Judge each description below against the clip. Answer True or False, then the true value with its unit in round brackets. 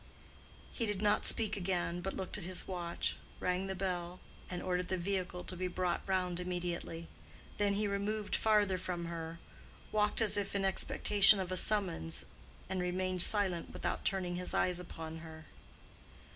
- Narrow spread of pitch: True (2.2 semitones)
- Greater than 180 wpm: False (165 wpm)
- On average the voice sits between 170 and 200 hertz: True (185 Hz)